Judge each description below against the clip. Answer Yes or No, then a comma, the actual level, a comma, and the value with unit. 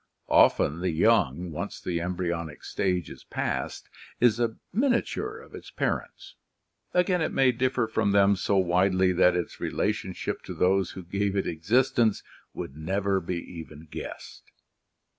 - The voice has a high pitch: No, very low, 95 Hz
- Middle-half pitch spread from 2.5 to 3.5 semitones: No, average, 4.7 semitones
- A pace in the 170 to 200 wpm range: No, average, 150 wpm